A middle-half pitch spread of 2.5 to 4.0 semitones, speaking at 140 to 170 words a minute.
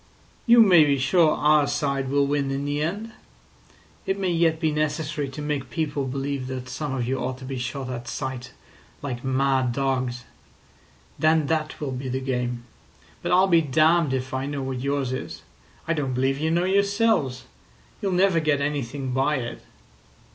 No: average, 3.2 semitones; average, 180 wpm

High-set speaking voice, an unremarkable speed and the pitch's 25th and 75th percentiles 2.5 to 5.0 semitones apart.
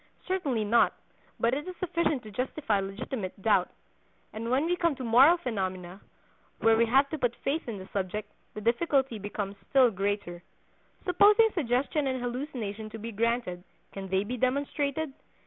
No: high, 235 Hz; average, 165 wpm; wide, 5.4 semitones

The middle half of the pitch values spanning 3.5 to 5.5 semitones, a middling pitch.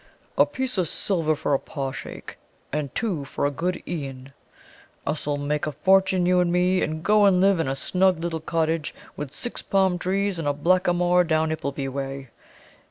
Yes: average, 4.2 semitones; medium, 165 Hz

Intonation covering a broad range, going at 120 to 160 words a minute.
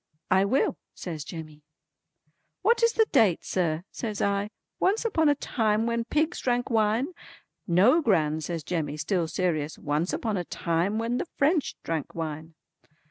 Yes: wide, 7.2 semitones; average, 155 wpm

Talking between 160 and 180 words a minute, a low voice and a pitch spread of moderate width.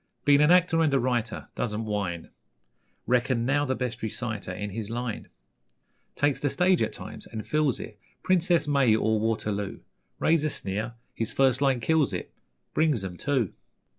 Yes: average, 165 wpm; low, 125 Hz; average, 5.0 semitones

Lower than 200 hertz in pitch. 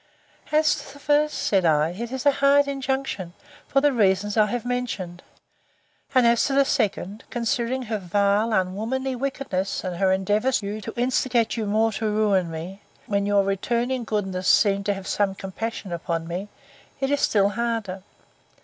No: high, 215 Hz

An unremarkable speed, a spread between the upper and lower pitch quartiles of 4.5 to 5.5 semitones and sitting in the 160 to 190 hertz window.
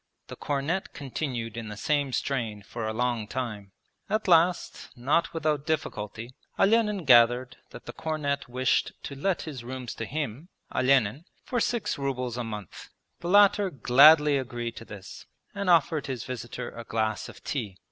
No: average, 160 wpm; average, 5.0 semitones; low, 130 Hz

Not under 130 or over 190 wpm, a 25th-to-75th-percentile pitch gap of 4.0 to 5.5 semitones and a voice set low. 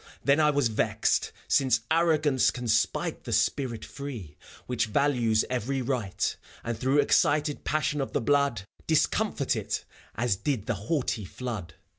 Yes: average, 145 wpm; average, 4.3 semitones; low, 125 Hz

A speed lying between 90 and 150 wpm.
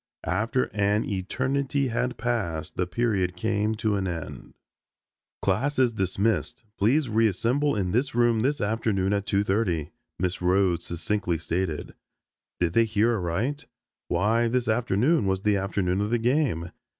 Yes: average, 140 wpm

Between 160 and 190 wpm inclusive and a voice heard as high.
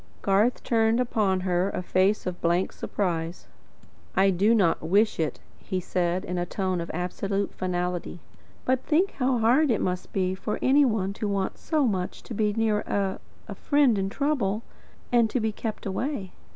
Yes: average, 180 wpm; high, 200 Hz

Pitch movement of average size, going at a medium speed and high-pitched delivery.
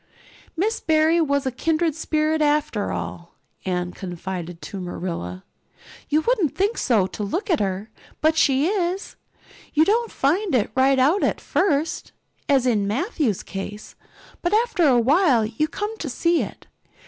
No: wide, 8.4 semitones; average, 155 wpm; very high, 285 Hz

